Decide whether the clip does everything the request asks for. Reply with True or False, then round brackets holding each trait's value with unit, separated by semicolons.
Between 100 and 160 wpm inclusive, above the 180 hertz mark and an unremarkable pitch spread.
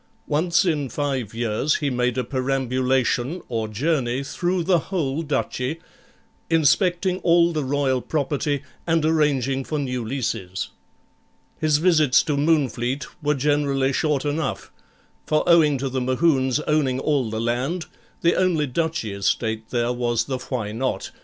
False (140 wpm; 140 Hz; 3.7 semitones)